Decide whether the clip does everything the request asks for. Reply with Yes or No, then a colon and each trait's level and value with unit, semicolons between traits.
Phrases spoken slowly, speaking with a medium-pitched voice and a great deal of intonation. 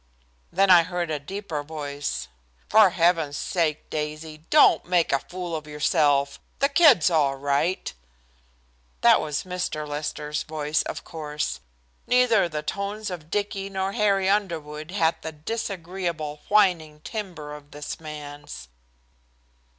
No: slow, 130 wpm; medium, 160 Hz; average, 4.3 semitones